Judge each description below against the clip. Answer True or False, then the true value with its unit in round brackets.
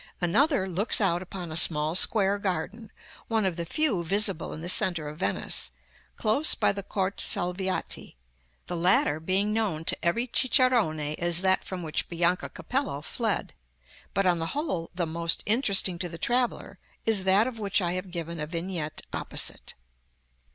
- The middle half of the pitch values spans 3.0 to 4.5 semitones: True (3.9 semitones)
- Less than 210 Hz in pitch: True (185 Hz)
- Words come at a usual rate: True (165 wpm)